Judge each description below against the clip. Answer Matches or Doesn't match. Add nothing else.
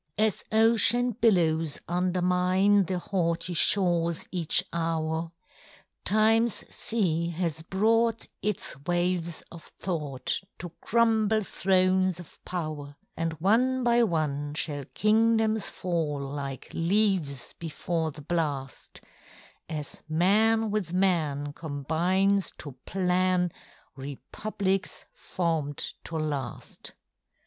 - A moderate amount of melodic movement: Matches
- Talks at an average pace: Doesn't match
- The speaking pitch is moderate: Matches